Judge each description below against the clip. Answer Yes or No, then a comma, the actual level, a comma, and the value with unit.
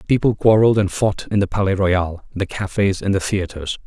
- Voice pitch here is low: Yes, low, 100 Hz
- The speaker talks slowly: No, average, 200 wpm